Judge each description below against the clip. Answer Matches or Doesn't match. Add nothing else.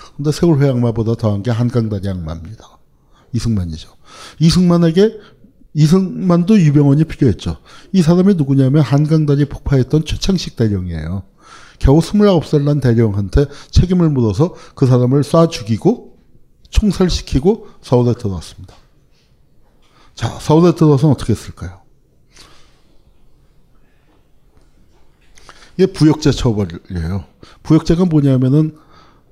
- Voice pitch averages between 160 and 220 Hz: Doesn't match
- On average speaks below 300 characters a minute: Matches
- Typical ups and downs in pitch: Doesn't match